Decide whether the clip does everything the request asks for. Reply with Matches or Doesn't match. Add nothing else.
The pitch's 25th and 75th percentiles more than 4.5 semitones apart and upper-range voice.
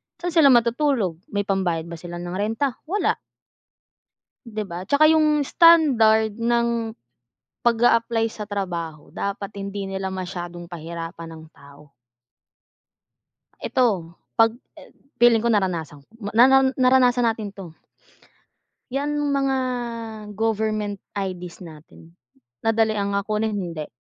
Matches